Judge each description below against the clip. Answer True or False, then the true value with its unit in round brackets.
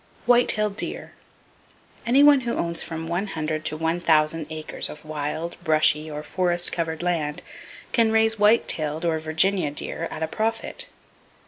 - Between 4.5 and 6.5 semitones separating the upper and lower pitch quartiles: True (5.0 semitones)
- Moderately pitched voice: True (165 Hz)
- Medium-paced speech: True (155 wpm)